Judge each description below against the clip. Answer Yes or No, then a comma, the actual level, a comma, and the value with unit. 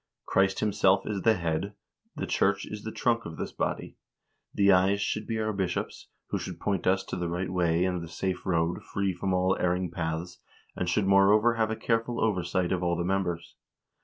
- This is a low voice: Yes, very low, 95 Hz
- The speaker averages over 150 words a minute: Yes, average, 200 wpm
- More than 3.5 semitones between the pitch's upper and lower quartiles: No, average, 2.8 semitones